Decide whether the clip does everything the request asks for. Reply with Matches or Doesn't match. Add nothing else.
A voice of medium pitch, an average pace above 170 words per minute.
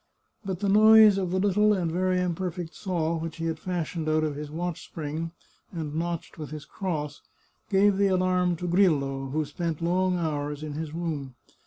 Matches